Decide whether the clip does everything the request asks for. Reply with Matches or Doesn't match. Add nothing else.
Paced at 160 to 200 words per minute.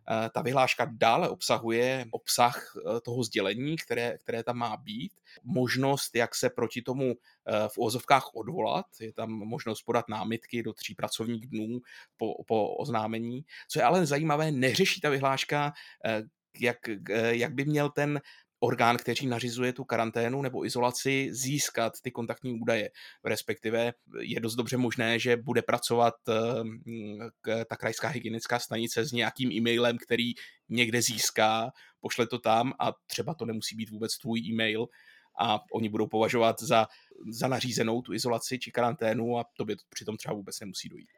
Doesn't match